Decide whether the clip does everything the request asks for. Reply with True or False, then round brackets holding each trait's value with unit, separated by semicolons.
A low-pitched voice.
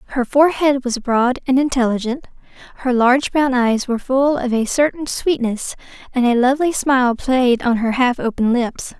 False (255 Hz)